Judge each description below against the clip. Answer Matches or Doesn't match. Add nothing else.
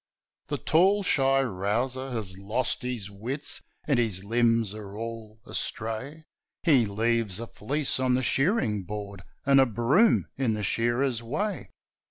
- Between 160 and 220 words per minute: Doesn't match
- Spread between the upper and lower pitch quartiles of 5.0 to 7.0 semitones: Doesn't match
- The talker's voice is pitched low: Matches